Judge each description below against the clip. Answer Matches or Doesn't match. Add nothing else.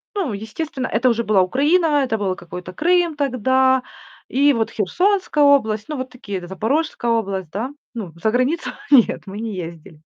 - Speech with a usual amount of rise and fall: Doesn't match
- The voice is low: Doesn't match